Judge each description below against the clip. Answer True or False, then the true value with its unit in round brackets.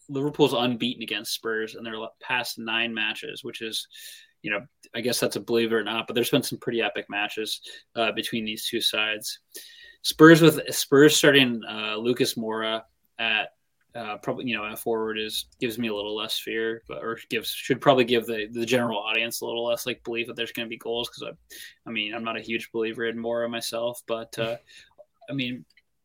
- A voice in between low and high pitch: False (115 Hz)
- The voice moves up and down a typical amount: False (2.0 semitones)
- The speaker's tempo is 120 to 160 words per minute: False (205 wpm)